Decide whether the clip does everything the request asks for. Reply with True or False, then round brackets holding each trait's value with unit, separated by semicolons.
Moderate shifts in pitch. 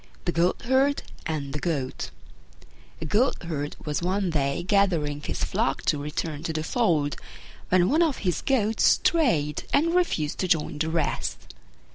False (6.0 semitones)